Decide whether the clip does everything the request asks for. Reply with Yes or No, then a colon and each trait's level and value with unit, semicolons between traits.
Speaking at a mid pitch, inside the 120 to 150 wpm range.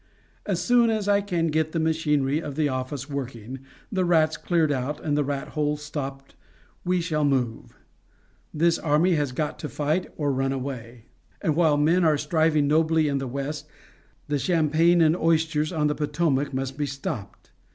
No: medium, 150 Hz; average, 175 wpm